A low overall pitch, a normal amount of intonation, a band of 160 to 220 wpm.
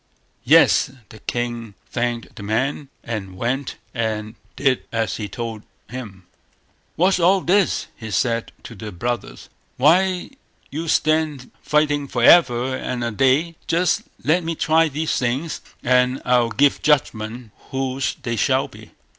No: low, 125 Hz; average, 4.8 semitones; average, 145 wpm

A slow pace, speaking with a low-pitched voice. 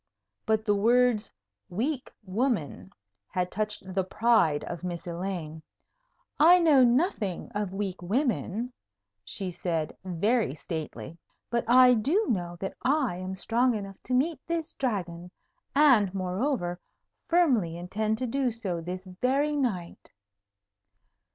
No: slow, 125 wpm; high, 210 Hz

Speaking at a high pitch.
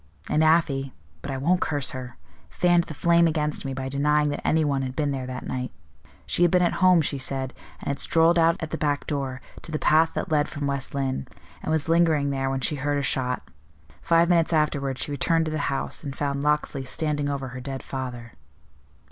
No: medium, 145 Hz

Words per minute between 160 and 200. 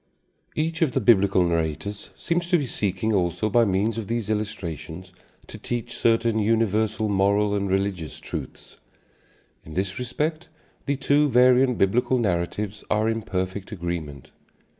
No: average, 140 wpm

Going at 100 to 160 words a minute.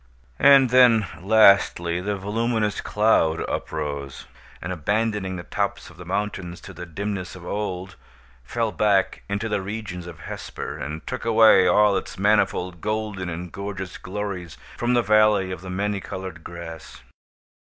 Yes: average, 150 wpm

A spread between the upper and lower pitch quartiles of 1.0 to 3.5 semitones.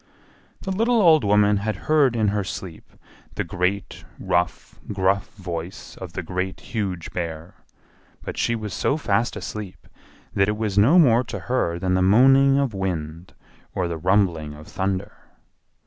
No: average, 3.9 semitones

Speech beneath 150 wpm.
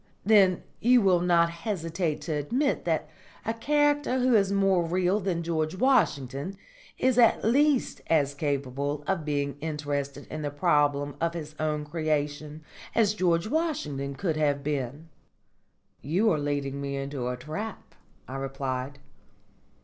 Yes: average, 140 wpm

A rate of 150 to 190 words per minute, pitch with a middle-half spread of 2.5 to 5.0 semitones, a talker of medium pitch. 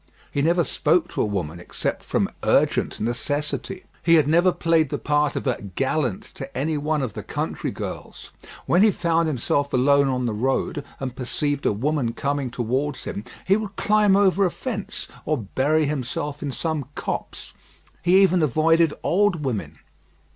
Yes: average, 170 wpm; average, 4.5 semitones; medium, 150 Hz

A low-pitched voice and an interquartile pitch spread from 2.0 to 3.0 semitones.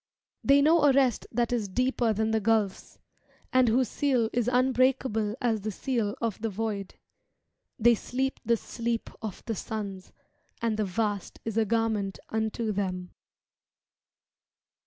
No: high, 225 Hz; average, 2.7 semitones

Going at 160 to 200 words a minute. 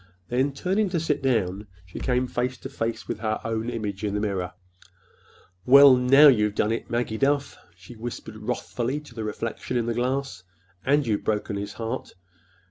Yes: average, 180 wpm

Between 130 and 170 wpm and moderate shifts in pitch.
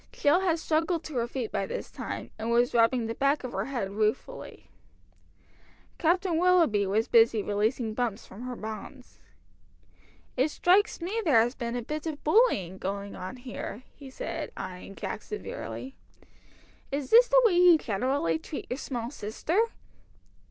No: average, 160 wpm; wide, 6.5 semitones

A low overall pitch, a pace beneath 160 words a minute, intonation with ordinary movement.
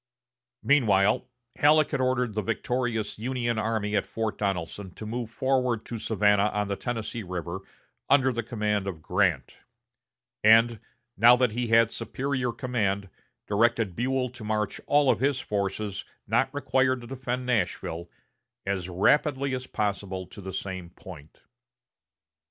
Yes: low, 115 Hz; average, 140 wpm; average, 3.9 semitones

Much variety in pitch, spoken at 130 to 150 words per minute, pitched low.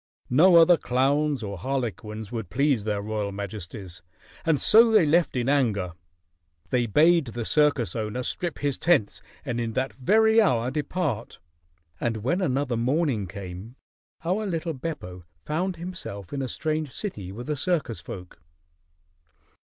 Yes: wide, 7.0 semitones; average, 145 wpm; low, 130 Hz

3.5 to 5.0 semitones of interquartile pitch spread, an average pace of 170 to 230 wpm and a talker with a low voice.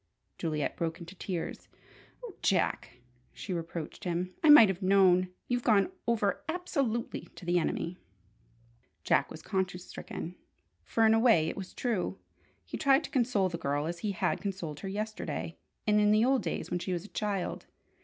No: average, 4.3 semitones; average, 175 wpm; high, 190 Hz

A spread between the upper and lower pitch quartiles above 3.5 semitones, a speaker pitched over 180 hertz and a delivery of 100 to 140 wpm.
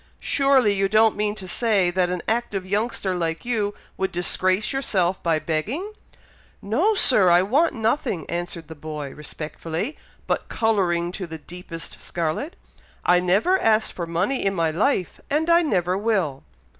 No: average, 4.6 semitones; high, 190 Hz; average, 155 wpm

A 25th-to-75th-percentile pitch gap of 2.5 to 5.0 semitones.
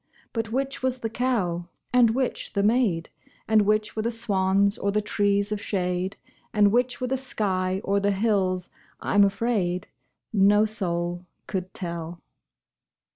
Yes: average, 3.4 semitones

